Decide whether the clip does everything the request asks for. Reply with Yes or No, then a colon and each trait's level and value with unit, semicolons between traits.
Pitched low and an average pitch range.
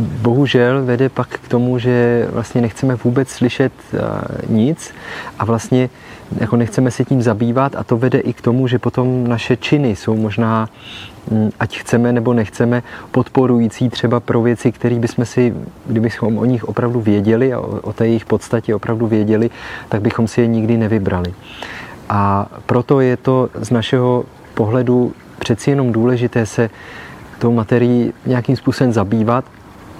No: low, 120 Hz; narrow, 1.8 semitones